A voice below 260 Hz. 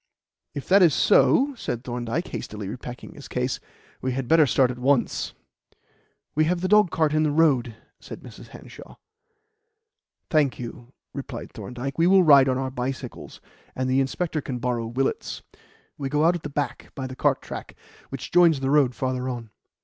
Yes: low, 135 Hz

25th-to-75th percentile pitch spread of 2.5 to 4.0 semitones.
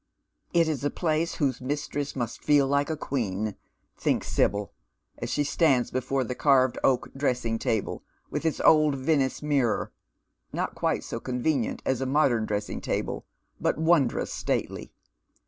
Yes: average, 3.3 semitones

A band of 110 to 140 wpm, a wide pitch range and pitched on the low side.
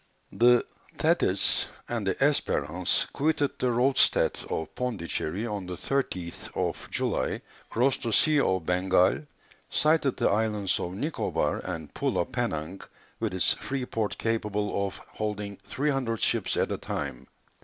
Yes: slow, 135 wpm; wide, 5.8 semitones; low, 105 Hz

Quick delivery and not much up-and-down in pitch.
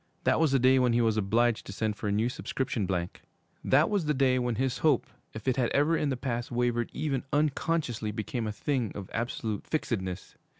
No: fast, 215 wpm; average, 3.8 semitones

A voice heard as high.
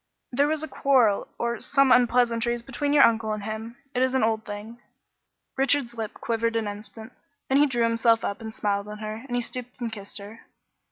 Yes: high, 230 Hz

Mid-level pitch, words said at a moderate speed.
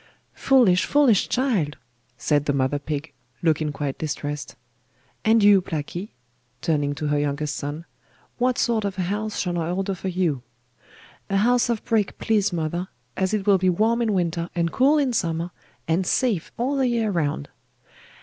Yes: medium, 180 Hz; average, 170 wpm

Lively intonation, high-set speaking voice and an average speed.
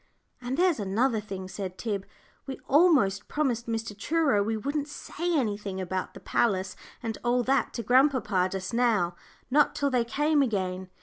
Yes: wide, 5.7 semitones; high, 230 Hz; average, 165 wpm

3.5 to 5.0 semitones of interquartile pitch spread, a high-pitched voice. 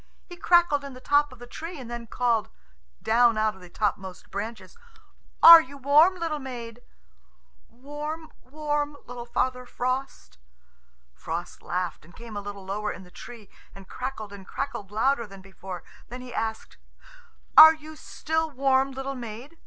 No: wide, 5.5 semitones; high, 245 Hz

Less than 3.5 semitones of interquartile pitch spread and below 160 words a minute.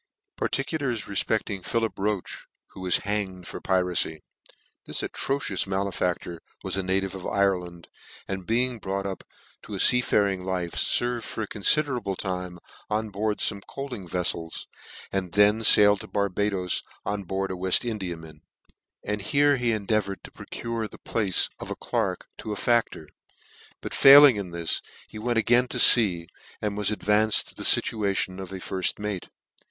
No: average, 3.0 semitones; average, 165 wpm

